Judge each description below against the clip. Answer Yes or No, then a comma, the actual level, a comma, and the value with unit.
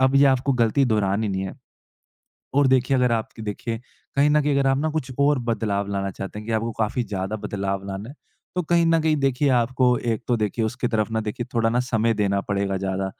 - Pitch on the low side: Yes, low, 115 Hz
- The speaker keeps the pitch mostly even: No, average, 4.5 semitones